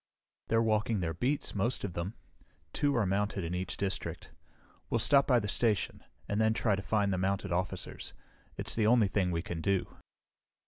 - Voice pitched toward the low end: Yes, low, 100 Hz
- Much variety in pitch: No, average, 3.3 semitones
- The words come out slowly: No, average, 185 wpm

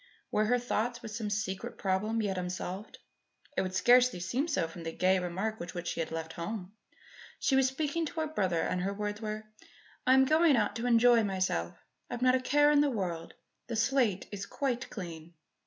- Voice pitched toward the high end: Yes, high, 215 Hz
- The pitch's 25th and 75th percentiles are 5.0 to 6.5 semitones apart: Yes, average, 5.3 semitones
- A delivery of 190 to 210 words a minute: Yes, fast, 205 wpm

